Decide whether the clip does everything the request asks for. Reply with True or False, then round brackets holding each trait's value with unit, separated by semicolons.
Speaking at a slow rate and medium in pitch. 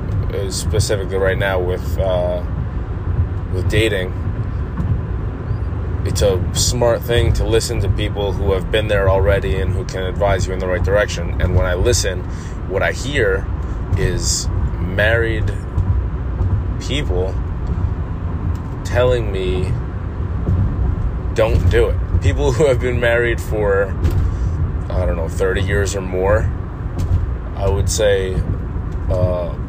False (125 wpm; 95 Hz)